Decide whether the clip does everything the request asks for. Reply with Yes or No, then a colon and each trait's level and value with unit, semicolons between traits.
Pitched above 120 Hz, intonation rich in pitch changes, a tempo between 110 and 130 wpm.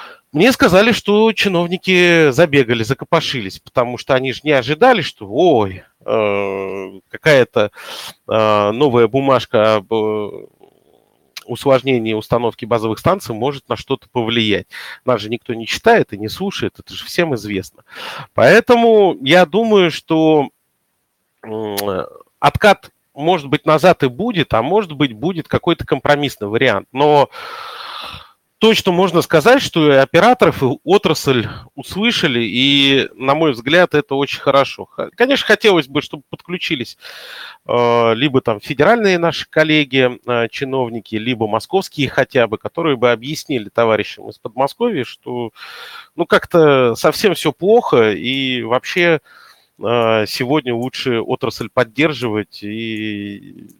Yes: low, 135 Hz; wide, 6.5 semitones; average, 120 wpm